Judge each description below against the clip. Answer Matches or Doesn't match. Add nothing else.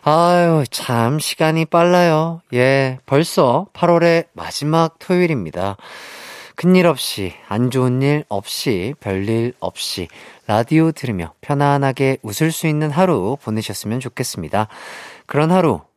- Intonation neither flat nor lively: Doesn't match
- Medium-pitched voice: Matches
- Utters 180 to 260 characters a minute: Matches